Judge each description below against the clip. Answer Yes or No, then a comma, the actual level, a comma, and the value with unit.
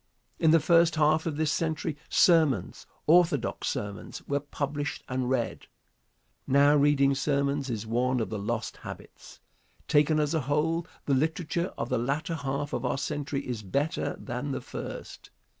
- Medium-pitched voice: Yes, medium, 145 Hz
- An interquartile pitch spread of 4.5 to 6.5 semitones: No, average, 3.0 semitones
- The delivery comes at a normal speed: Yes, average, 160 wpm